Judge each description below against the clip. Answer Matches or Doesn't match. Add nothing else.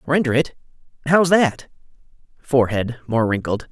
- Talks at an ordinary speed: Doesn't match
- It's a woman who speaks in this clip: Doesn't match